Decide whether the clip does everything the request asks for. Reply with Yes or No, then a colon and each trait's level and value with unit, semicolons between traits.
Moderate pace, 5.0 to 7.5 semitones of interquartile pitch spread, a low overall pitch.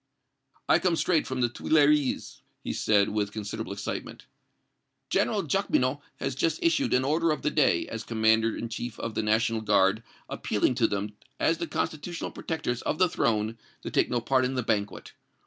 Yes: average, 180 wpm; wide, 5.5 semitones; low, 120 Hz